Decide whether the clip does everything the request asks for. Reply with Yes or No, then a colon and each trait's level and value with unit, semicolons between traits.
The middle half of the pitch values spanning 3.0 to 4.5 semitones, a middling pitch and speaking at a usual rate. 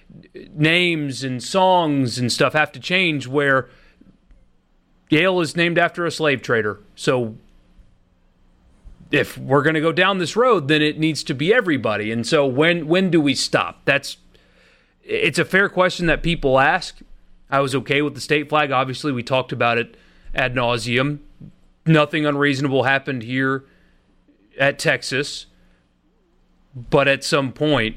Yes: average, 4.1 semitones; medium, 145 Hz; average, 150 wpm